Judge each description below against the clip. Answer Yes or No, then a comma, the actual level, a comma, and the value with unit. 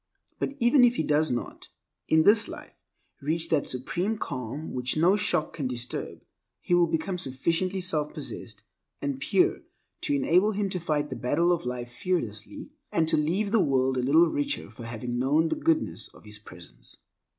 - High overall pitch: No, medium, 155 Hz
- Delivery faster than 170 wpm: Yes, average, 180 wpm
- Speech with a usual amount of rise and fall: No, wide, 6.2 semitones